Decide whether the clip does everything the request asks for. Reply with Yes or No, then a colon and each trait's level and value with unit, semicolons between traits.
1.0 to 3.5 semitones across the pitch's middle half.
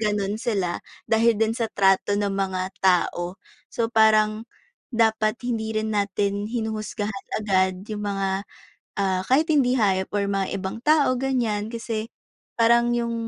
Yes: average, 2.7 semitones